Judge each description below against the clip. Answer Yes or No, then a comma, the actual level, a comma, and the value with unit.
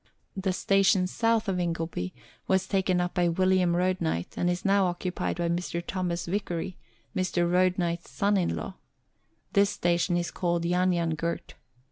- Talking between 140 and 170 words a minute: Yes, average, 160 wpm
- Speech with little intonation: Yes, narrow, 1.6 semitones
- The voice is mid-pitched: Yes, medium, 180 Hz